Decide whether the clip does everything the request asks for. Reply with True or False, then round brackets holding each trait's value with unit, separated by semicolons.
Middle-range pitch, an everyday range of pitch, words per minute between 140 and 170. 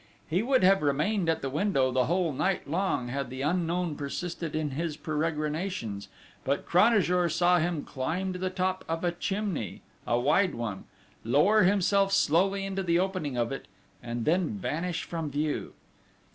True (170 Hz; 4.5 semitones; 165 wpm)